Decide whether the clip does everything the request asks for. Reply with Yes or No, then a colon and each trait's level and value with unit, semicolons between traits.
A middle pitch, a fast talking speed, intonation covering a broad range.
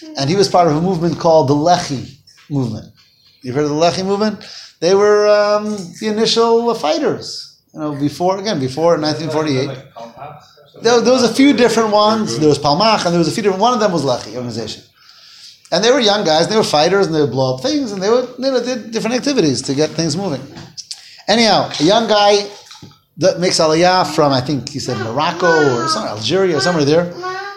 Yes: medium, 175 Hz; fast, 210 wpm; wide, 6.5 semitones